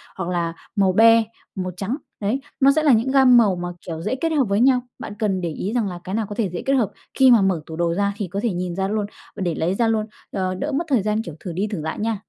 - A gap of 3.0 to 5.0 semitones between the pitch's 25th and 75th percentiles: Yes, average, 4.4 semitones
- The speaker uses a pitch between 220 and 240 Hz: No, high, 205 Hz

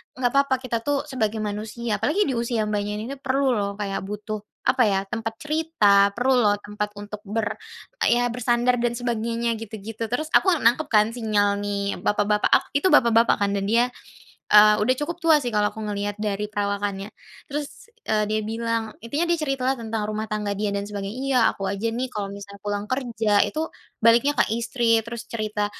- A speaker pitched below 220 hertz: No, high, 225 Hz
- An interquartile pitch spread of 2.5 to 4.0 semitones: Yes, average, 3.0 semitones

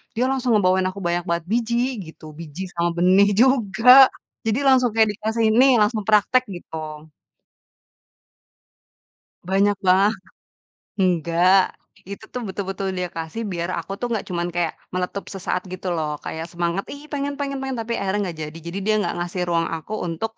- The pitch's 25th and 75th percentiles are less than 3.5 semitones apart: No, average, 4.4 semitones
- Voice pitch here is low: No, high, 195 Hz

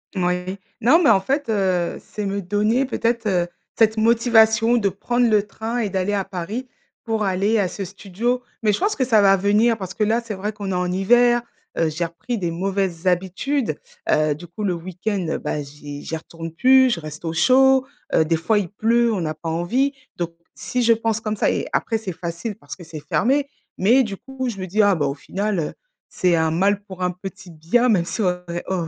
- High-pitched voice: Yes, high, 200 Hz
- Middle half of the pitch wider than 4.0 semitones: Yes, average, 4.4 semitones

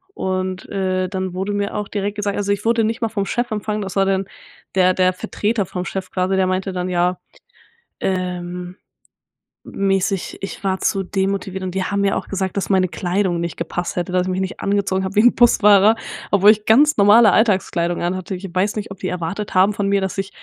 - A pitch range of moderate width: No, narrow, 1.7 semitones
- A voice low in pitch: No, high, 195 Hz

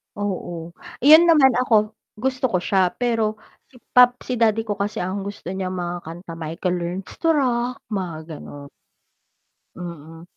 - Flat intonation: No, wide, 5.5 semitones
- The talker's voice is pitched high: Yes, high, 200 Hz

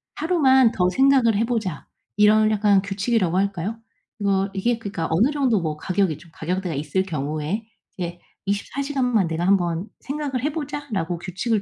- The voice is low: No, high, 200 Hz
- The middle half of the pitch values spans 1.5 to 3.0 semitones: No, average, 5.3 semitones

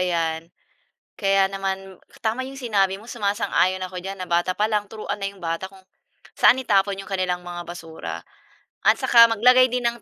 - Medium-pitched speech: No, high, 195 Hz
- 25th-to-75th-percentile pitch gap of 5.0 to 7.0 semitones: No, average, 3.1 semitones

